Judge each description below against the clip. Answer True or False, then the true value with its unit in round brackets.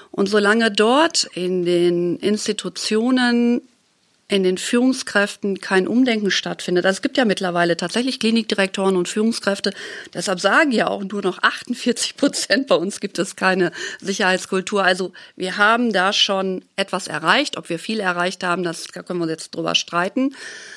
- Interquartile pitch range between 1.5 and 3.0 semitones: False (3.8 semitones)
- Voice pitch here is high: True (200 Hz)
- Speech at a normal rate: True (155 wpm)